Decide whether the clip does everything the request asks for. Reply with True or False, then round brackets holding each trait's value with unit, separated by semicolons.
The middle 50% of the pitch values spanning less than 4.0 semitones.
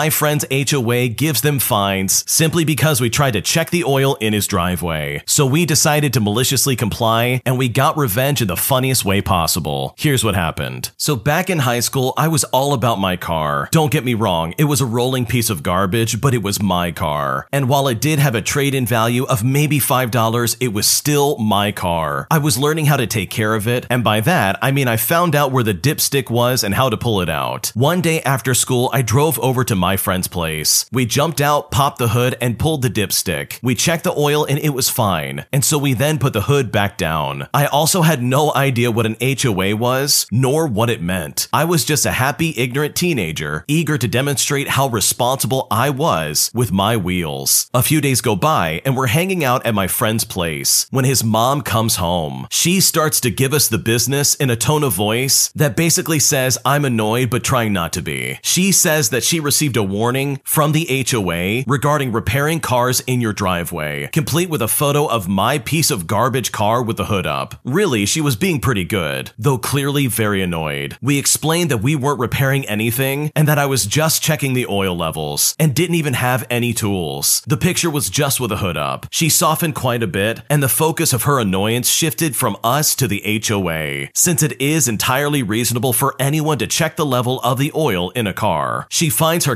False (5.1 semitones)